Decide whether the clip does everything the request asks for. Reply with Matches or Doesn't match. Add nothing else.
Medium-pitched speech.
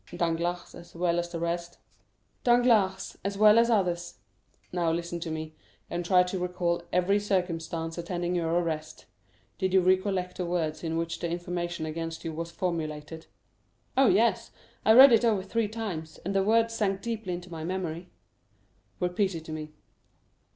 Matches